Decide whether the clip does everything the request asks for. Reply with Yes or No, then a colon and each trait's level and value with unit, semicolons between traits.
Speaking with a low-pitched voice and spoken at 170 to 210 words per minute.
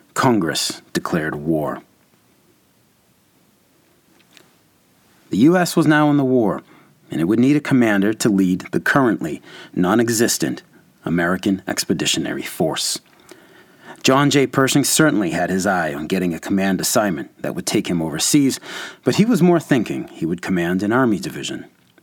No: low, 125 Hz; average, 145 wpm